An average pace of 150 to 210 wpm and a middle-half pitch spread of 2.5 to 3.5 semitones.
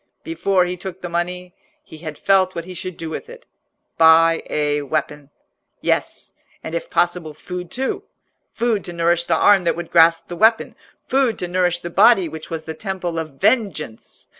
Yes: average, 180 wpm; average, 2.8 semitones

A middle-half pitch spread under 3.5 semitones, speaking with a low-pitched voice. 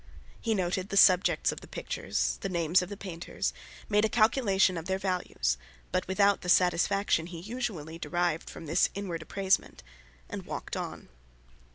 No: average, 2.8 semitones; medium, 185 Hz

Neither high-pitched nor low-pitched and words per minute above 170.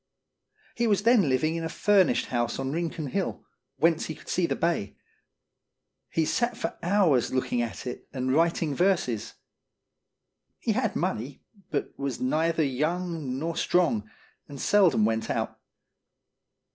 No: medium, 160 Hz; average, 145 wpm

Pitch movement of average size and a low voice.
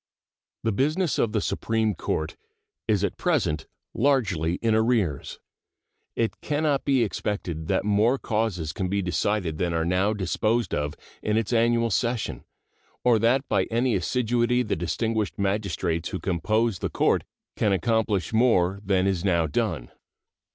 Yes: average, 4.3 semitones; low, 105 Hz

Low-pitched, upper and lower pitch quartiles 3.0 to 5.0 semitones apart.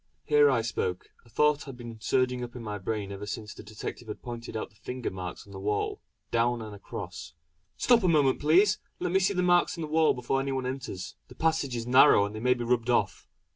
No: low, 125 Hz; wide, 5.4 semitones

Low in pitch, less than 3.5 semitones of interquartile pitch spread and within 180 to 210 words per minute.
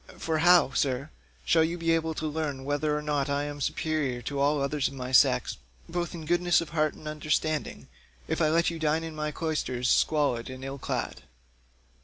No: medium, 150 Hz; narrow, 2.4 semitones; average, 195 wpm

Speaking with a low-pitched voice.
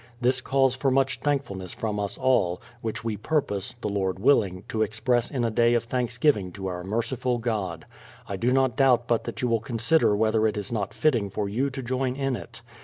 Yes: low, 115 Hz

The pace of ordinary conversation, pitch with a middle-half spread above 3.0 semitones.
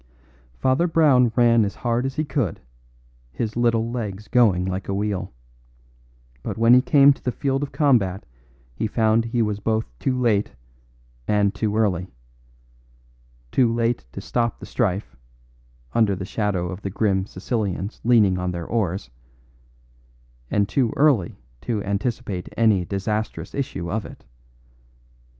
Yes: average, 145 wpm; average, 3.7 semitones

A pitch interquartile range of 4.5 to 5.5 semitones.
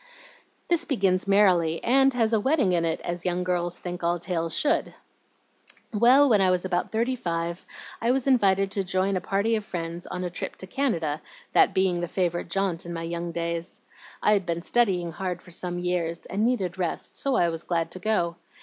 No: average, 3.5 semitones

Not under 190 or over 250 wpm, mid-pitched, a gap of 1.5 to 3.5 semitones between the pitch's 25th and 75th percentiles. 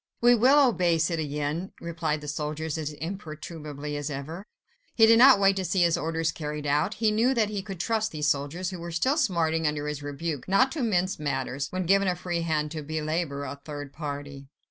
No: average, 195 wpm; medium, 165 Hz; average, 4.4 semitones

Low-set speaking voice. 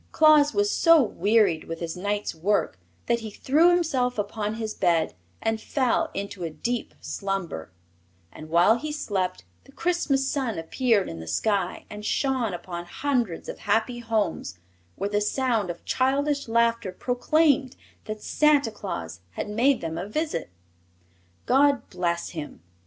No: high, 220 Hz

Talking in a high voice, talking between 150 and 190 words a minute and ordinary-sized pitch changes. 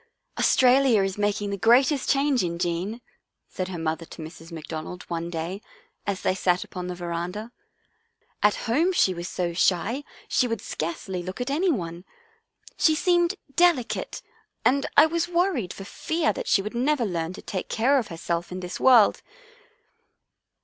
No: high, 200 Hz; average, 170 wpm; wide, 7.6 semitones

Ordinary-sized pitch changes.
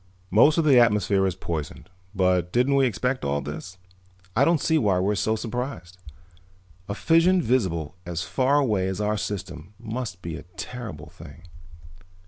No: wide, 5.9 semitones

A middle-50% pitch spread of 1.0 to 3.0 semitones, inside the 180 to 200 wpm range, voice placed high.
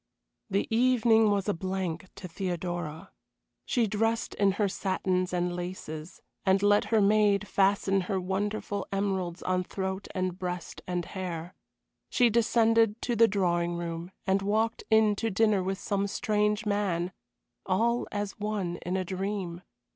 No: narrow, 2.5 semitones; average, 145 wpm; high, 195 Hz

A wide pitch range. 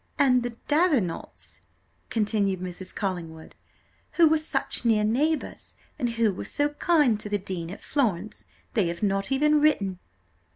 Yes: wide, 7.2 semitones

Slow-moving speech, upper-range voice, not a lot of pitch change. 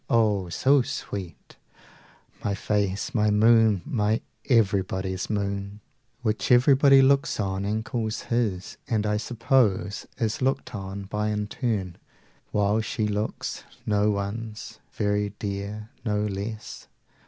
No: slow, 125 wpm; low, 105 Hz; narrow, 2.1 semitones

